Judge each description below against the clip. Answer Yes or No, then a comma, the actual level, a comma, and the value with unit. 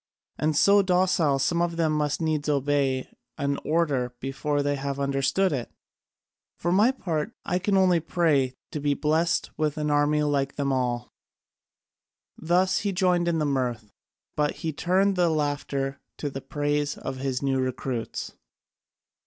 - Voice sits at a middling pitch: Yes, medium, 150 Hz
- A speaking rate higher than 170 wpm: No, average, 155 wpm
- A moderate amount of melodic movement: Yes, average, 3.8 semitones